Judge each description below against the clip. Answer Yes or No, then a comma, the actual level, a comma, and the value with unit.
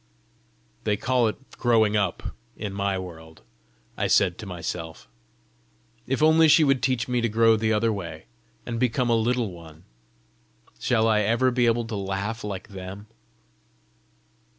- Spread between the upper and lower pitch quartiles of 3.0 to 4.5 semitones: Yes, average, 3.7 semitones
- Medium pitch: No, low, 110 Hz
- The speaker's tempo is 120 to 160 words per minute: Yes, average, 150 wpm